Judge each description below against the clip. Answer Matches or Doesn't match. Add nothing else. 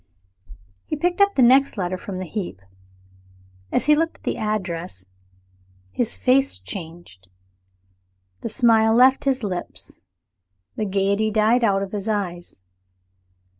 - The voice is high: Matches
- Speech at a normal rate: Doesn't match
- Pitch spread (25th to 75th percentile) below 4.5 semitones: Doesn't match